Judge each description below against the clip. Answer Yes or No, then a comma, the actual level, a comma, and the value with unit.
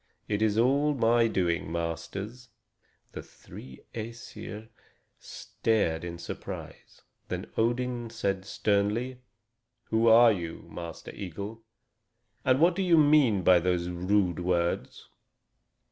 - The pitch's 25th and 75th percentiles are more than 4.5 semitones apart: Yes, average, 5.2 semitones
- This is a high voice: No, low, 105 Hz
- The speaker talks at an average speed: No, slow, 115 wpm